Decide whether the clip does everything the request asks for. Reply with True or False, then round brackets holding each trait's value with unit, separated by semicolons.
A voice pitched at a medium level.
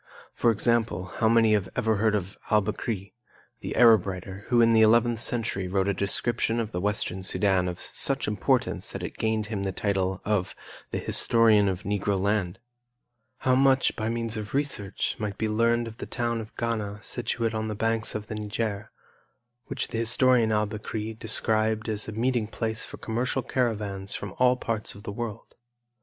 False (110 Hz)